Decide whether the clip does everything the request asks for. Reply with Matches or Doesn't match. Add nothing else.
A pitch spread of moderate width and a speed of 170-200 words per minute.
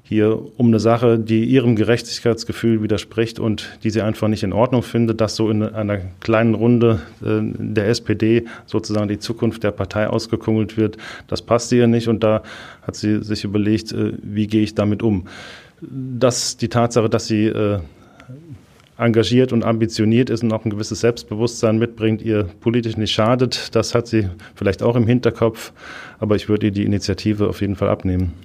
Doesn't match